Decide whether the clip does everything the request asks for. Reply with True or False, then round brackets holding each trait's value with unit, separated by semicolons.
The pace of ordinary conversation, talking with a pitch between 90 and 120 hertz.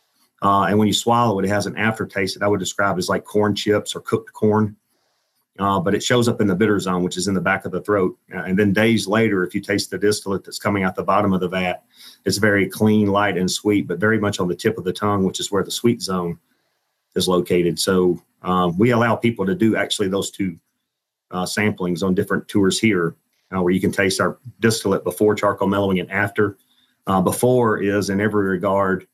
False (235 wpm; 100 Hz)